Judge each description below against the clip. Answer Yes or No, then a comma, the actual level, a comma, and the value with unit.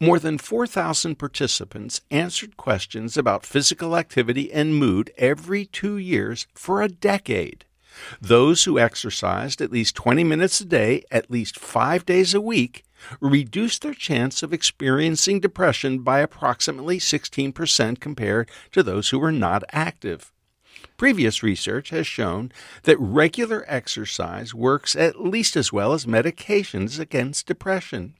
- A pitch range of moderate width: No, wide, 6.7 semitones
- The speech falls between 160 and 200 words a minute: No, slow, 135 wpm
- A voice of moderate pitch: Yes, medium, 150 Hz